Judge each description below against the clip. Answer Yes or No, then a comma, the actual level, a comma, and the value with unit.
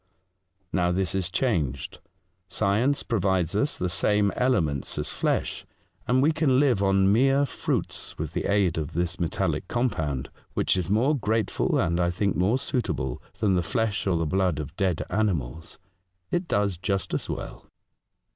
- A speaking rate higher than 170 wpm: No, average, 165 wpm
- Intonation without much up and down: No, average, 4.5 semitones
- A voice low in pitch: Yes, very low, 95 Hz